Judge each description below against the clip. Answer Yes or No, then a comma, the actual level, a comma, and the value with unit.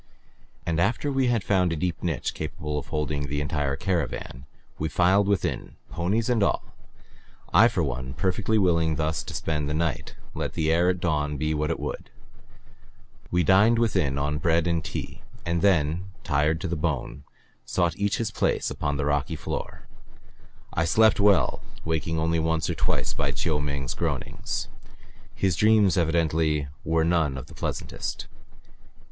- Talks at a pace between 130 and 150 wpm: No, average, 165 wpm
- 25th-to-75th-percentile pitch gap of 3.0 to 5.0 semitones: Yes, average, 3.8 semitones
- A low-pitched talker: Yes, very low, 80 Hz